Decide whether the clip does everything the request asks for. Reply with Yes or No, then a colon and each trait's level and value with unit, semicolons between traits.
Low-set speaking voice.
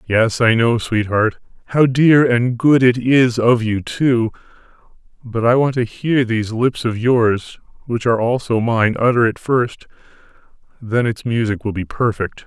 Yes: low, 115 Hz